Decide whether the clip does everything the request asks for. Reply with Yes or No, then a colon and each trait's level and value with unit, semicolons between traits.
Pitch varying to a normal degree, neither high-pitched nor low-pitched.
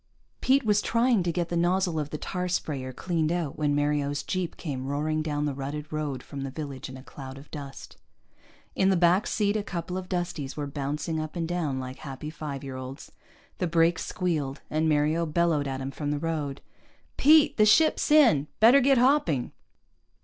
Yes: average, 4.1 semitones; medium, 155 Hz